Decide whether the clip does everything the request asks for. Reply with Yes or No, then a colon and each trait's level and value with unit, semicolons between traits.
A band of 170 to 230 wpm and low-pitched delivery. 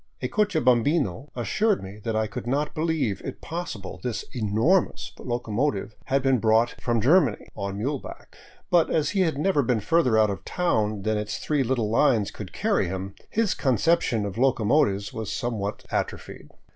Yes: average, 180 wpm; low, 120 Hz